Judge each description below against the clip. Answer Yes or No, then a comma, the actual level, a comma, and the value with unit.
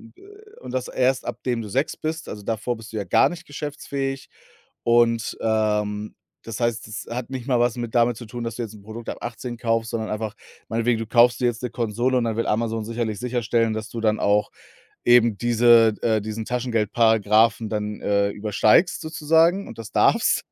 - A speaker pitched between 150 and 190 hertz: No, low, 115 Hz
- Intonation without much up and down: Yes, narrow, 2.1 semitones